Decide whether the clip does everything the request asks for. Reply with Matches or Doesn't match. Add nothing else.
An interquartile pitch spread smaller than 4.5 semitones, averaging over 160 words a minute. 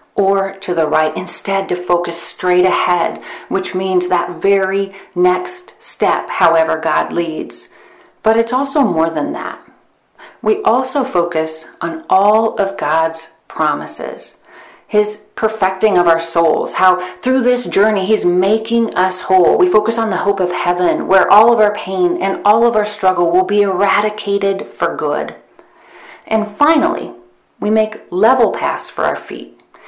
Doesn't match